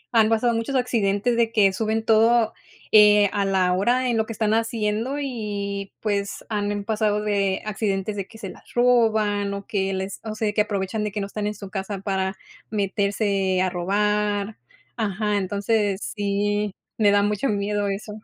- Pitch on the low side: No, high, 210 Hz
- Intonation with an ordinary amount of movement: No, narrow, 1.8 semitones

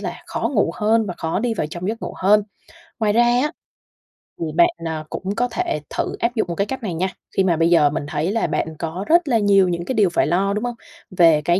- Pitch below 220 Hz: Yes, high, 195 Hz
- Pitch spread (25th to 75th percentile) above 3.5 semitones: Yes, average, 5.0 semitones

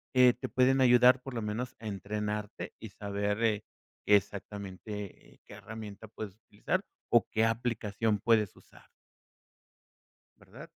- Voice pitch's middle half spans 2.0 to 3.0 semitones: Yes, narrow, 2.4 semitones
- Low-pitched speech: Yes, low, 110 Hz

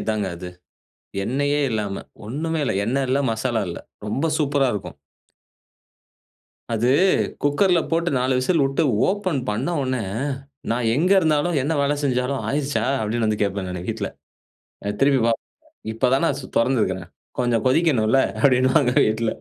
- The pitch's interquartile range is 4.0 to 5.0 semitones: Yes, average, 4.6 semitones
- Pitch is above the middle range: No, low, 130 Hz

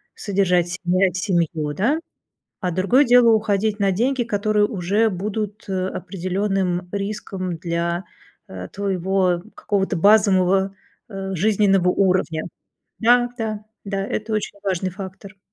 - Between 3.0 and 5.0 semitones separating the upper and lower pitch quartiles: No, narrow, 2.5 semitones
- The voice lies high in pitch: Yes, high, 195 Hz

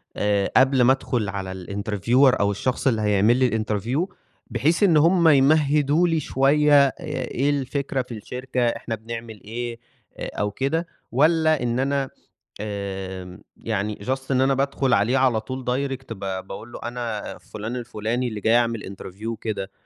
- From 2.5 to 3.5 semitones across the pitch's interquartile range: No, average, 4.2 semitones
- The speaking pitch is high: No, low, 120 Hz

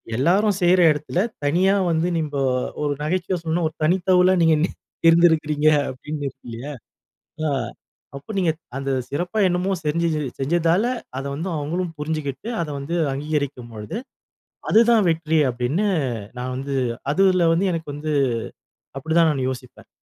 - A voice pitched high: No, medium, 160 Hz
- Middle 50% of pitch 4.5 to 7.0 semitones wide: No, average, 3.7 semitones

